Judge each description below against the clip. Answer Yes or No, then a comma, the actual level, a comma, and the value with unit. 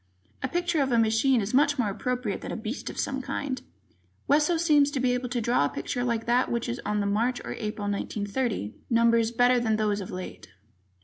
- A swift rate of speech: Yes, fast, 210 wpm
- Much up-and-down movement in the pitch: No, average, 3.5 semitones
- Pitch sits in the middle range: No, high, 240 Hz